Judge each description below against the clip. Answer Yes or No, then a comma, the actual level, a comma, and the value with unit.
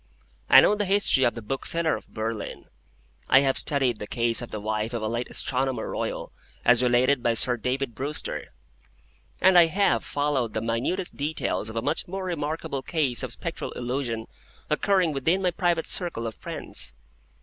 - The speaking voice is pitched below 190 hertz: Yes, low, 135 Hz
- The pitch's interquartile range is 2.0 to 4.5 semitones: No, wide, 5.6 semitones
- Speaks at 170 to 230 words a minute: Yes, average, 175 wpm